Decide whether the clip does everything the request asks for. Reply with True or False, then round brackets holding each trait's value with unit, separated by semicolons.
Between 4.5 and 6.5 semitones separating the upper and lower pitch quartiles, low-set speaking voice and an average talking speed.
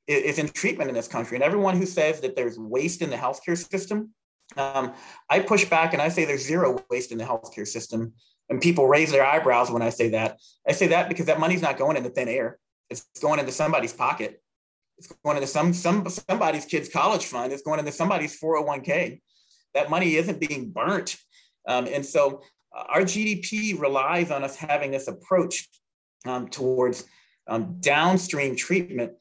False (5.4 semitones; 155 Hz; 190 wpm)